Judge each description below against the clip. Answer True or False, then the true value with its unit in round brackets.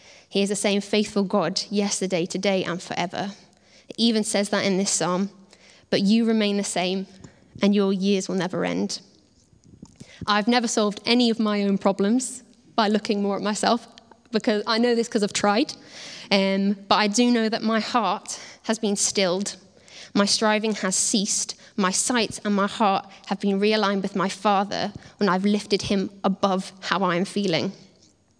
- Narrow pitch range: True (2.0 semitones)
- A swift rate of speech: False (175 wpm)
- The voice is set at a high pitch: True (205 Hz)